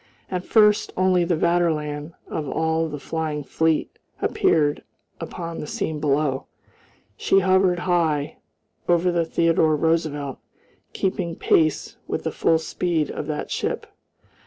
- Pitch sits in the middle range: Yes, medium, 160 Hz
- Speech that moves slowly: Yes, slow, 130 wpm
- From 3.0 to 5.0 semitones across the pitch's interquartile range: No, narrow, 2.6 semitones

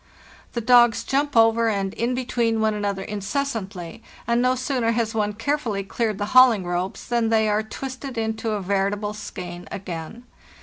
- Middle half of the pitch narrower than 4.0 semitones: Yes, average, 3.1 semitones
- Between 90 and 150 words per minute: No, average, 165 wpm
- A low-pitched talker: No, high, 220 Hz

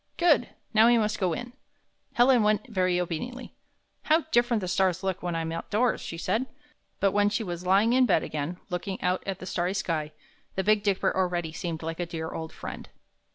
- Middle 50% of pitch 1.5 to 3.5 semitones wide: No, average, 4.2 semitones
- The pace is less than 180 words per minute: No, average, 200 wpm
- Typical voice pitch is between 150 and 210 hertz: Yes, high, 190 Hz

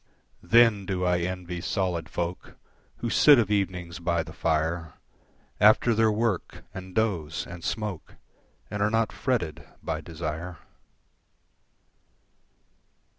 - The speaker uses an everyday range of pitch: Yes, average, 4.0 semitones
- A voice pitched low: Yes, very low, 90 Hz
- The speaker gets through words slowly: Yes, slow, 120 wpm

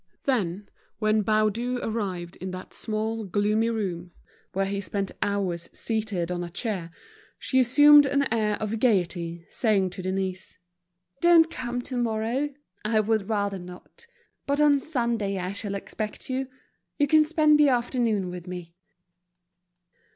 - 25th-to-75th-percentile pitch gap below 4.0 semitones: No, average, 4.8 semitones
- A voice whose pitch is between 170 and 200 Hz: No, high, 215 Hz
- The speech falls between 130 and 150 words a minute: Yes, slow, 135 wpm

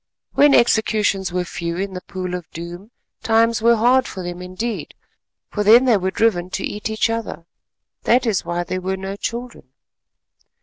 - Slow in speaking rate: No, average, 170 wpm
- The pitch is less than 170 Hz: No, high, 195 Hz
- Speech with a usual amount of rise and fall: Yes, average, 4.0 semitones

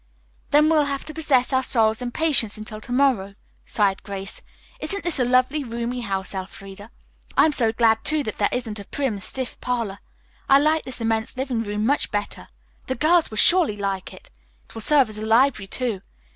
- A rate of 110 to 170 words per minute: No, average, 195 wpm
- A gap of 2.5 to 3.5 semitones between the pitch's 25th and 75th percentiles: No, average, 4.7 semitones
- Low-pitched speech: No, high, 235 Hz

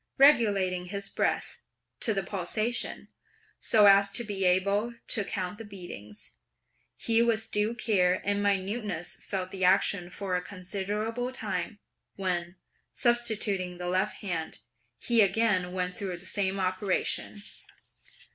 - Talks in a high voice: Yes, high, 200 Hz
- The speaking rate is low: Yes, slow, 130 wpm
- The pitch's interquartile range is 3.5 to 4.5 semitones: No, average, 2.8 semitones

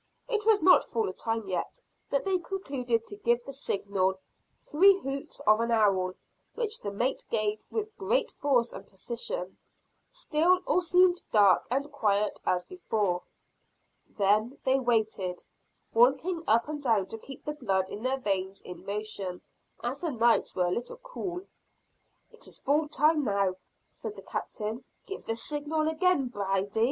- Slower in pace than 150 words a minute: No, average, 160 wpm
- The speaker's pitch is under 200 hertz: No, high, 240 Hz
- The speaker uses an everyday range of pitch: No, wide, 7.4 semitones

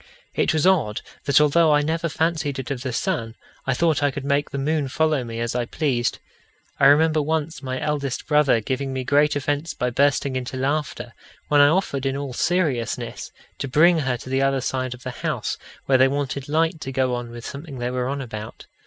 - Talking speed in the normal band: No, fast, 210 wpm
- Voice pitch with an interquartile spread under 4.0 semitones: Yes, average, 2.8 semitones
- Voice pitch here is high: No, medium, 140 Hz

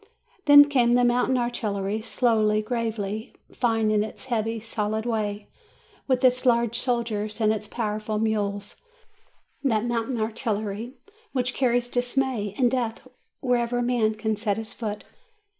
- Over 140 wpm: No, slow, 135 wpm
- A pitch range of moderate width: No, narrow, 2.3 semitones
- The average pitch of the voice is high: Yes, high, 225 Hz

